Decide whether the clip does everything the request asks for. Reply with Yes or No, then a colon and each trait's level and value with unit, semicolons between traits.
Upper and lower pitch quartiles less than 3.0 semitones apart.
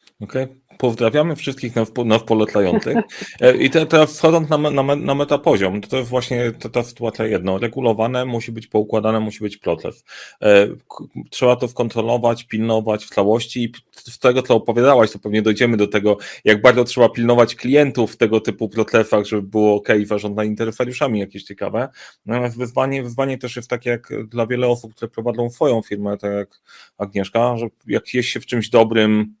Yes: narrow, 2.6 semitones